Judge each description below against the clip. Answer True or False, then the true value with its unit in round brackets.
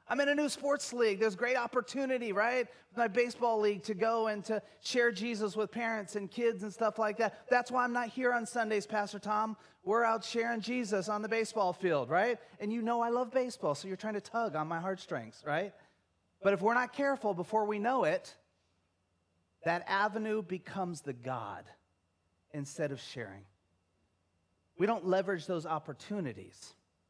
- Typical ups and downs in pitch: False (7.2 semitones)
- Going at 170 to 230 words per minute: True (180 wpm)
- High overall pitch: True (210 Hz)